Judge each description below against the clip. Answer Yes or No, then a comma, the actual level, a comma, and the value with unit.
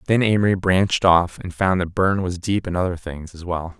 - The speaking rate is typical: No, fast, 235 wpm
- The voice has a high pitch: No, very low, 90 Hz